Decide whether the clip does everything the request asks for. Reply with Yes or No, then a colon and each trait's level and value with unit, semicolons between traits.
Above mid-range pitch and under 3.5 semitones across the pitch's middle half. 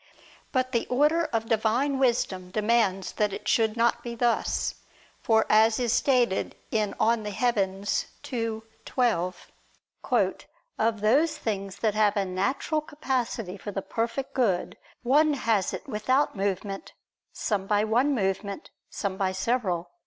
No: high, 220 Hz; average, 3.8 semitones